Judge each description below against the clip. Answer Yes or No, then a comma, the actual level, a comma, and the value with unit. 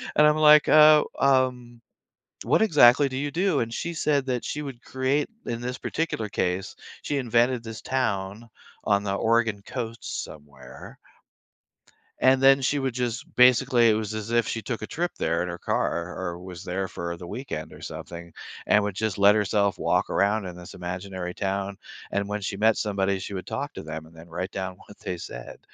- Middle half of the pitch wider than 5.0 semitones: Yes, wide, 5.6 semitones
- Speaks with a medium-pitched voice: No, low, 110 Hz